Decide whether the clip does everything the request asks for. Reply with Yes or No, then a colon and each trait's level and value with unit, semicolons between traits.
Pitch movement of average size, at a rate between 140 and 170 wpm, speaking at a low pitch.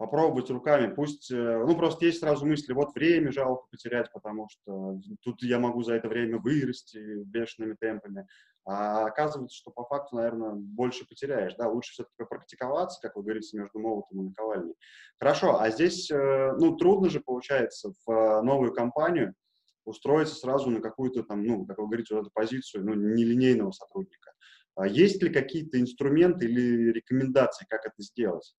Yes: average, 4.2 semitones; fast, 160 wpm; low, 120 Hz